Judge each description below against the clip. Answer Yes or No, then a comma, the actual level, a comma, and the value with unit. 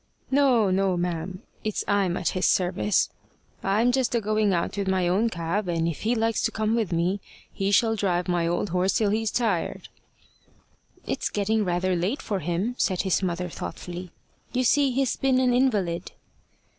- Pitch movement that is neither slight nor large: Yes, average, 3.9 semitones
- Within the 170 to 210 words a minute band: Yes, average, 180 wpm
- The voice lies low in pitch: No, high, 195 Hz